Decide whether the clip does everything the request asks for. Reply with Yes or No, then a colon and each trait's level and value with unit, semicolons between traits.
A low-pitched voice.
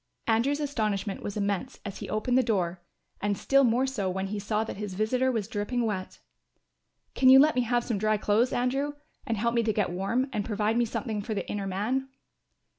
No: high, 220 Hz